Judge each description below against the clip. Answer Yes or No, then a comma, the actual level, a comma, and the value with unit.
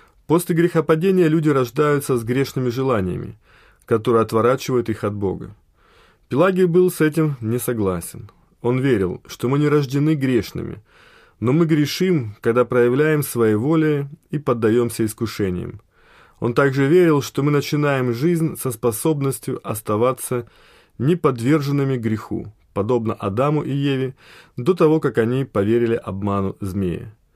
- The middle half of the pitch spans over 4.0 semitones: Yes, average, 5.1 semitones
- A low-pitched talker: Yes, low, 130 Hz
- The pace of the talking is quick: No, average, 125 wpm